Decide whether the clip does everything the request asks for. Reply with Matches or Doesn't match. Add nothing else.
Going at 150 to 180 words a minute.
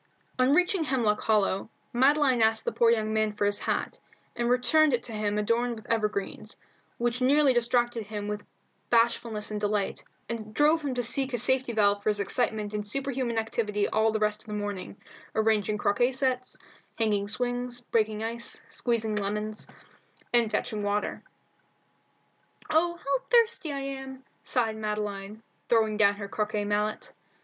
Matches